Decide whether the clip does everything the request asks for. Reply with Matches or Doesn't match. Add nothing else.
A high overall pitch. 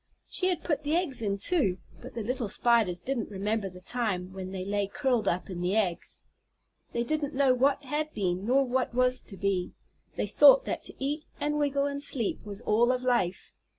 Matches